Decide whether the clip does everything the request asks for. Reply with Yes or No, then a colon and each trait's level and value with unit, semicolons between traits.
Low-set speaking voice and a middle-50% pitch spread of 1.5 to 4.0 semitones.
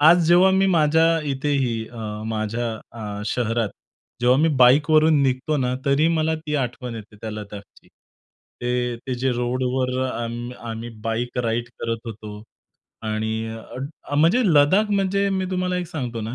No: low, 125 Hz; wide, 5.4 semitones